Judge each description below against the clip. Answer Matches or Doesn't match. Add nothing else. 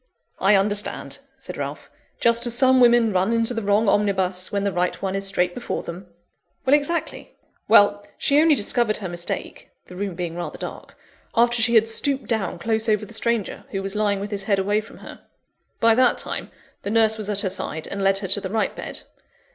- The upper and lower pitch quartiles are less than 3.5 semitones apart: Matches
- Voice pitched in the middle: Doesn't match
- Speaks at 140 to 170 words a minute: Doesn't match